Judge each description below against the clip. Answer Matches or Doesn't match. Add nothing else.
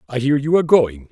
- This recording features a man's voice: Matches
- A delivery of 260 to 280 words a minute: Matches